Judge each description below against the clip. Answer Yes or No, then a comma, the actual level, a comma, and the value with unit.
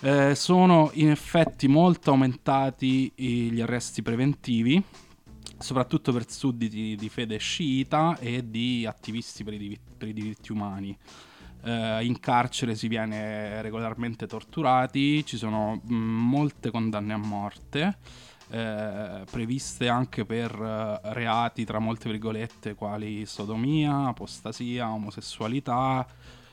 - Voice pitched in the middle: No, low, 115 Hz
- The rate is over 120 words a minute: No, slow, 115 wpm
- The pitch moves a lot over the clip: No, average, 3.2 semitones